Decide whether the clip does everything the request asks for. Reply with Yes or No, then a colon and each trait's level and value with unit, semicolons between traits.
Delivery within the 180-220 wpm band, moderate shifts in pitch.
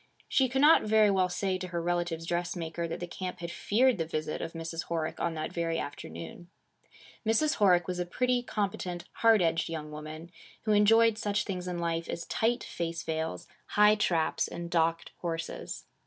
Yes: average, 185 wpm; average, 4.0 semitones